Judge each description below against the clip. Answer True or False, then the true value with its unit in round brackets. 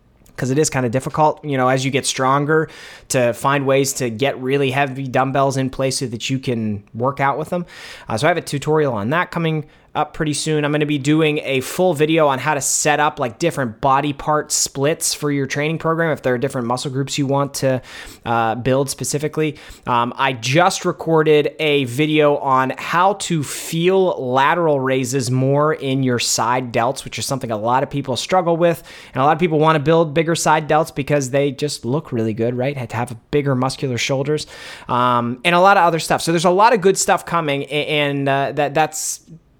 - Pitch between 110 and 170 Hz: True (140 Hz)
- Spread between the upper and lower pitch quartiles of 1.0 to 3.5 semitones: True (3.0 semitones)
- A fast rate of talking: True (220 wpm)